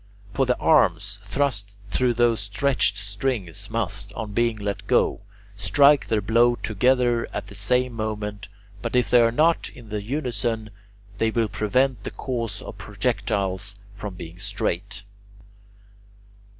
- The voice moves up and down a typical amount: Yes, average, 3.5 semitones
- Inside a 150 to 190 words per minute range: No, slow, 135 wpm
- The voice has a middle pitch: No, low, 110 Hz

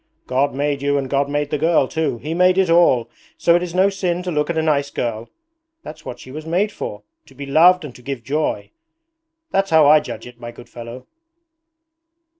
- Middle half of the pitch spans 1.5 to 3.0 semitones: No, average, 4.3 semitones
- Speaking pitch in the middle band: Yes, medium, 150 Hz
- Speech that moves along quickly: Yes, fast, 220 wpm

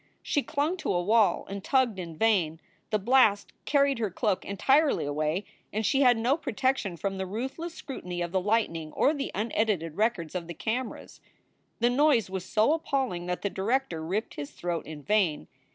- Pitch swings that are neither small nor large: No, wide, 6.7 semitones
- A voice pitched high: Yes, high, 210 Hz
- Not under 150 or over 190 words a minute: Yes, average, 185 wpm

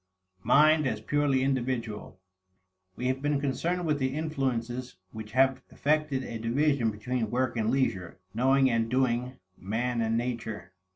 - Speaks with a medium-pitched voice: No, low, 130 Hz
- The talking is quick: No, average, 140 wpm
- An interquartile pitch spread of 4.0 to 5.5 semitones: No, average, 3.1 semitones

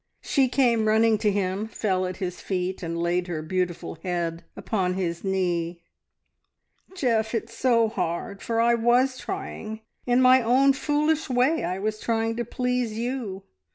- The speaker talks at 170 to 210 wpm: No, average, 155 wpm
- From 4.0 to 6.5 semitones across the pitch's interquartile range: Yes, average, 5.1 semitones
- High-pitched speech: Yes, high, 220 Hz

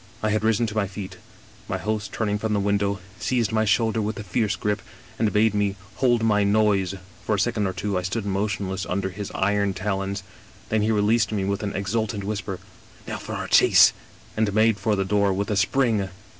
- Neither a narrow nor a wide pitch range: No, narrow, 1.7 semitones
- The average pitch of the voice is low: Yes, low, 105 Hz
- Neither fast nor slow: No, fast, 230 wpm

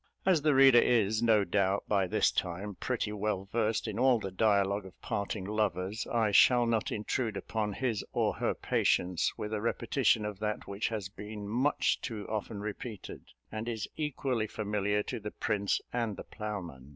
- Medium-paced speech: Yes, average, 175 wpm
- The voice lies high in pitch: No, low, 105 Hz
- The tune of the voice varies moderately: No, narrow, 2.3 semitones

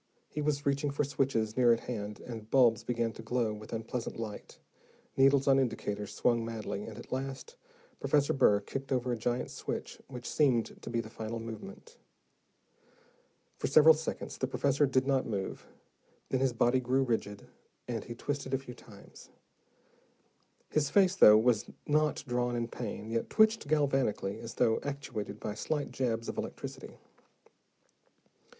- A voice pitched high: No, low, 125 Hz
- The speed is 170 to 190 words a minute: No, average, 155 wpm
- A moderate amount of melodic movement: Yes, average, 3.4 semitones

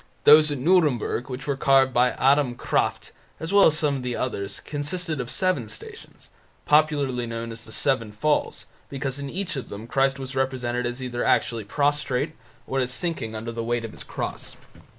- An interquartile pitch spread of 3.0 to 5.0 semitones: Yes, average, 3.4 semitones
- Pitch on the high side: No, low, 130 Hz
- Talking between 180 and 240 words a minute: Yes, average, 190 wpm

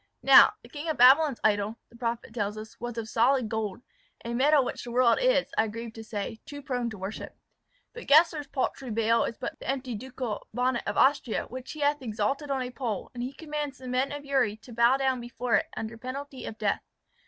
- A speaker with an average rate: No, fast, 220 wpm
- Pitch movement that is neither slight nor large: Yes, average, 3.4 semitones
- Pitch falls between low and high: No, high, 245 Hz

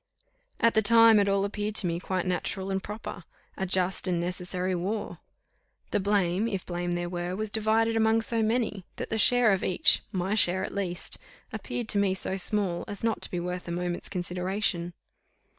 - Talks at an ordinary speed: Yes, average, 190 wpm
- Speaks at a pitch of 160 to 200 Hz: Yes, high, 190 Hz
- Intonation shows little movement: No, average, 3.2 semitones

